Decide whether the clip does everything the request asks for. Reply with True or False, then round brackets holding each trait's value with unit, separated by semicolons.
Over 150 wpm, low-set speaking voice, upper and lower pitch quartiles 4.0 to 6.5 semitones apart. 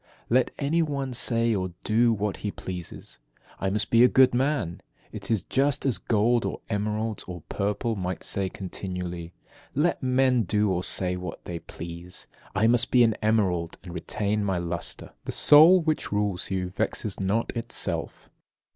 True (175 wpm; 105 Hz; 4.8 semitones)